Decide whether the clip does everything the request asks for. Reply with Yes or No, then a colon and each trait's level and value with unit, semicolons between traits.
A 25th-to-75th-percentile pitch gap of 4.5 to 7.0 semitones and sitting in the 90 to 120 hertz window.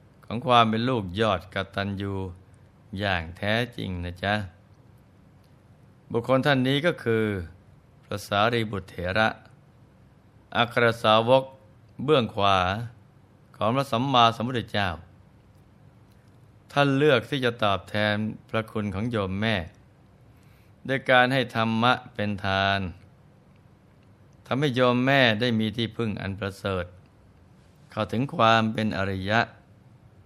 No: average, 3.6 semitones; low, 110 Hz